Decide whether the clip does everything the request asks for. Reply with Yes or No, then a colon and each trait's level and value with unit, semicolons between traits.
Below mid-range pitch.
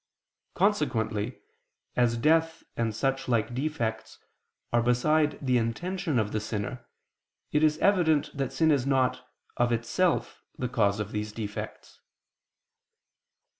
Yes: low, 125 Hz